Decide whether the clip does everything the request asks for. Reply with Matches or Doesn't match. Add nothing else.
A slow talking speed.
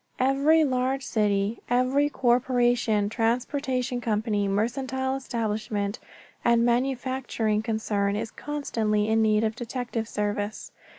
Matches